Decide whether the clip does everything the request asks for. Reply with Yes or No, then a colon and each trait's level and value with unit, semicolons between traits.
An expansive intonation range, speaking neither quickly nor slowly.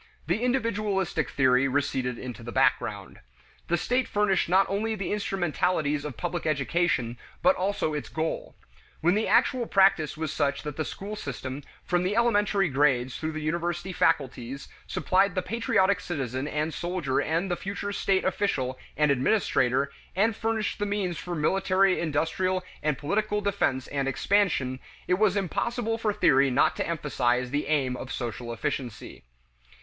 Yes: wide, 6.3 semitones; average, 155 wpm